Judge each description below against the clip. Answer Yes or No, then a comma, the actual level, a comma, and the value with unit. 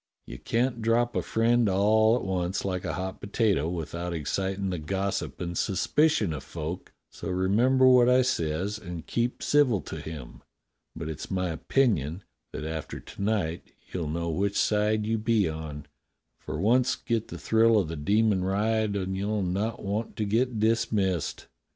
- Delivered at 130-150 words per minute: No, average, 170 wpm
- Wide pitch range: No, average, 4.5 semitones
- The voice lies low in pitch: Yes, low, 100 Hz